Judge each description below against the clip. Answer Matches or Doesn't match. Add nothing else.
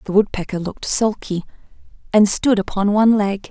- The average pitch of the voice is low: Doesn't match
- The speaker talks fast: Doesn't match